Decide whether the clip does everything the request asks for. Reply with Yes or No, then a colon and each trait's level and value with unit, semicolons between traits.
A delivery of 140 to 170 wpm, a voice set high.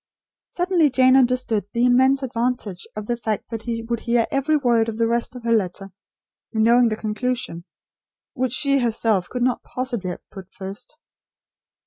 Yes: average, 165 wpm; high, 235 Hz